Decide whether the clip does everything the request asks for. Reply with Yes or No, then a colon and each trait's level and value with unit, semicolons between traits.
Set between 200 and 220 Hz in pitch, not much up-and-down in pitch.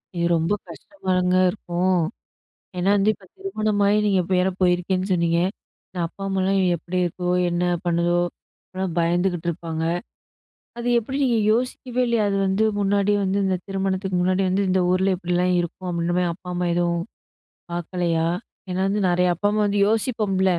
No: medium, 185 Hz; narrow, 2.3 semitones